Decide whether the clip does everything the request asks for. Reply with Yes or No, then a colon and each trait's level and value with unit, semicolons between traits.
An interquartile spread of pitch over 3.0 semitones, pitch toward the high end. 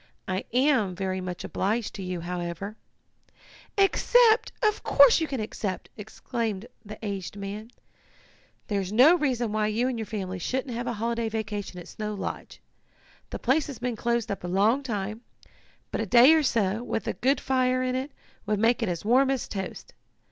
Yes: average, 4.3 semitones; high, 220 Hz